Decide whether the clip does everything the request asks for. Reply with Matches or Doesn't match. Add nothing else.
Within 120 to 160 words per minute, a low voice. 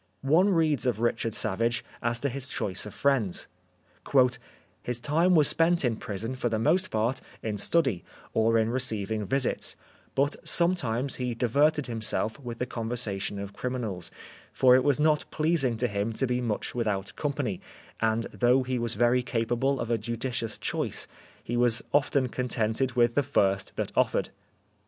Doesn't match